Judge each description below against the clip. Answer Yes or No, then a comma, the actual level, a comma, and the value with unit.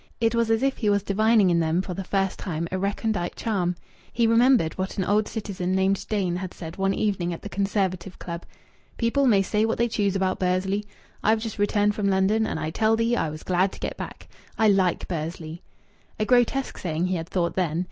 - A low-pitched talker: No, high, 195 Hz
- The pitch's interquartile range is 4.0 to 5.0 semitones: No, average, 3.4 semitones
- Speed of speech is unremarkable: No, fast, 220 wpm